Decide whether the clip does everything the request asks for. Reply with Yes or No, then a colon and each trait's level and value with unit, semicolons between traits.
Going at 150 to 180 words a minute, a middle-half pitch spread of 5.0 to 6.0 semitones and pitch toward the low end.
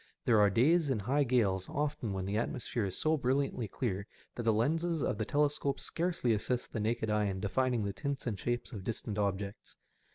No: average, 200 wpm; average, 5.3 semitones; low, 115 Hz